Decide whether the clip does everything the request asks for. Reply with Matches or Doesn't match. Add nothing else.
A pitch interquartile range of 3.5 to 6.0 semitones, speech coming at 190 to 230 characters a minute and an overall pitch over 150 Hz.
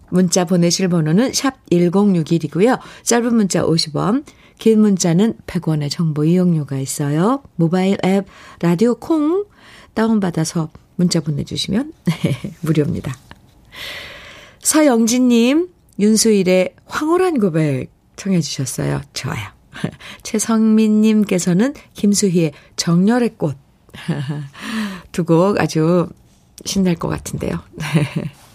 Matches